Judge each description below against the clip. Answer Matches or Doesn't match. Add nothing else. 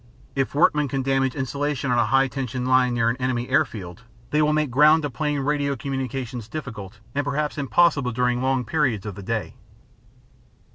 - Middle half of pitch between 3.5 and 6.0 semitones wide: Doesn't match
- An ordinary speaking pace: Matches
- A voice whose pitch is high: Doesn't match